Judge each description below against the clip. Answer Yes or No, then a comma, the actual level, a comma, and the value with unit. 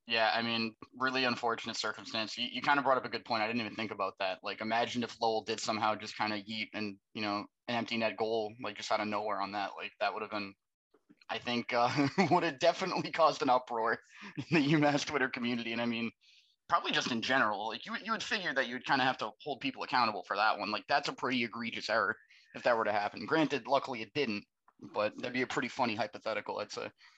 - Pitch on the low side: Yes, low, 115 Hz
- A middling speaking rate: No, fast, 245 wpm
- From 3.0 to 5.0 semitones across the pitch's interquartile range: Yes, average, 3.7 semitones